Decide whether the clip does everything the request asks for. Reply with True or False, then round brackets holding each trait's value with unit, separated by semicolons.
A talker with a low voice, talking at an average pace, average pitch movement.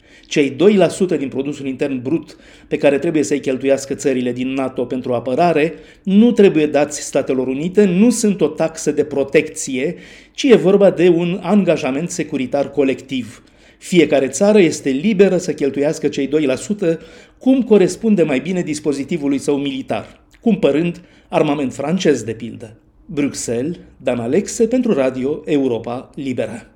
False (150 Hz; 140 wpm; 5.0 semitones)